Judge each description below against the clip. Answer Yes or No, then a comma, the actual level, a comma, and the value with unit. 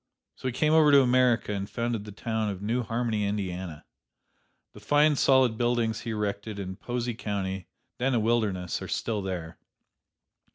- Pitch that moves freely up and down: No, average, 3.4 semitones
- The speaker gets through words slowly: No, average, 165 wpm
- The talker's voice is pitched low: Yes, low, 110 Hz